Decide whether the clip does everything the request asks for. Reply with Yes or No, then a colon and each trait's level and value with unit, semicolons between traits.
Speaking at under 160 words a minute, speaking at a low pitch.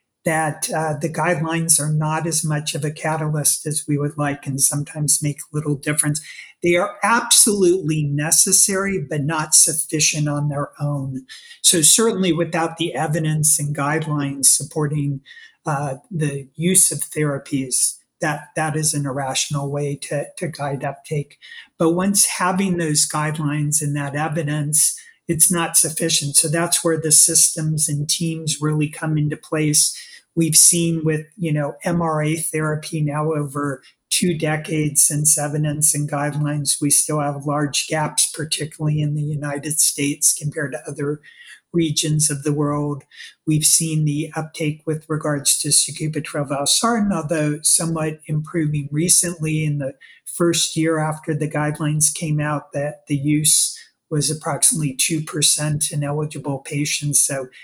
No: average, 145 wpm; medium, 155 Hz